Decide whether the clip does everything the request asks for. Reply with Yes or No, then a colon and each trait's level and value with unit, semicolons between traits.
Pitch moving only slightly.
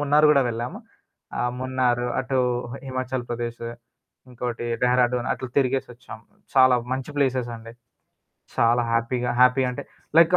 Yes: narrow, 1.5 semitones